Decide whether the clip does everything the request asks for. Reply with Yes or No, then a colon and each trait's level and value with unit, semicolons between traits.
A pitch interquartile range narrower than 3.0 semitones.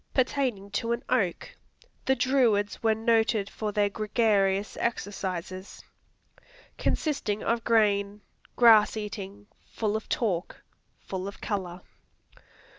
Yes: narrow, 2.5 semitones